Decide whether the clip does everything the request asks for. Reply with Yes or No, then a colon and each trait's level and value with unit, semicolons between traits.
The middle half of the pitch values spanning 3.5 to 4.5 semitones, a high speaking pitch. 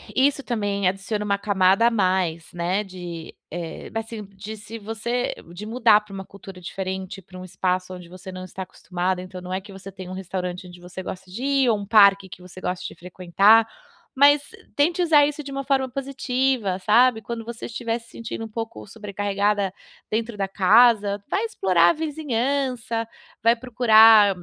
Yes: average, 4.1 semitones; high, 205 Hz